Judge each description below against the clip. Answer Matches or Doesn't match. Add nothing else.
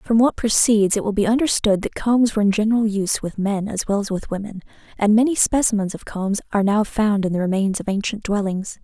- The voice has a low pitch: Doesn't match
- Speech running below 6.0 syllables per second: Doesn't match